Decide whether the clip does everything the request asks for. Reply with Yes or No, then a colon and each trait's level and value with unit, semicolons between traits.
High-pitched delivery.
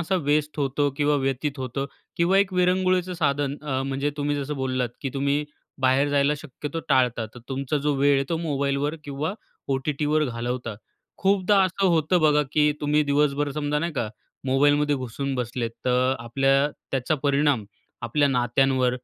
No: medium, 140 Hz